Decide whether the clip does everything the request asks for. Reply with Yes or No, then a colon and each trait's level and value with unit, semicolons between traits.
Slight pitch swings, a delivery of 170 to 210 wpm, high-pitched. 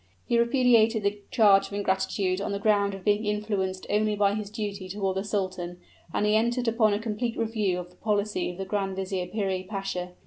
Yes: narrow, 2.1 semitones; fast, 205 wpm; high, 205 Hz